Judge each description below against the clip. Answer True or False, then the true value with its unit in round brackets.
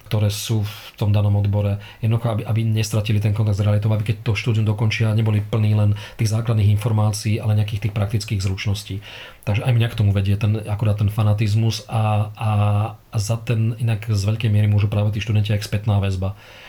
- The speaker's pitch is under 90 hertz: False (105 Hz)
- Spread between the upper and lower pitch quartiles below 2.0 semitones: True (1.2 semitones)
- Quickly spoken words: True (200 wpm)